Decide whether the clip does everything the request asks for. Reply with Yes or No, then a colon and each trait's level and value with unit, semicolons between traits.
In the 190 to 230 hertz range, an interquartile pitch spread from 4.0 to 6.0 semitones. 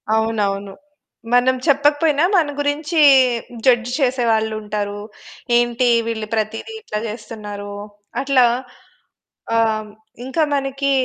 No: high, 240 Hz; average, 4.4 semitones